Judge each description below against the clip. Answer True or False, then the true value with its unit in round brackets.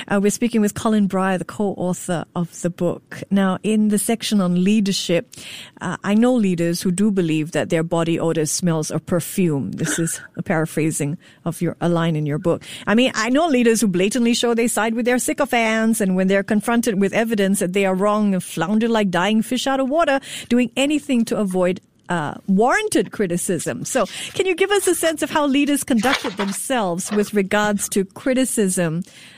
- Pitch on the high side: True (200 Hz)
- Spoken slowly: False (195 wpm)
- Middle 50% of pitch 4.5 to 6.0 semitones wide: True (5.1 semitones)